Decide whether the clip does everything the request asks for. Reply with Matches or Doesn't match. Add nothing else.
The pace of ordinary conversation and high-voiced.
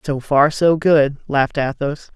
Doesn't match